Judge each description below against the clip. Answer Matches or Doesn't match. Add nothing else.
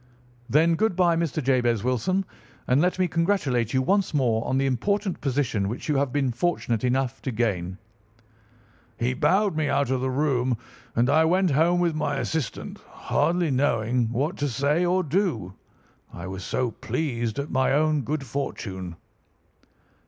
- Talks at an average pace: Matches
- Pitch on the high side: Doesn't match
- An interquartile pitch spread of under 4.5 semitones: Doesn't match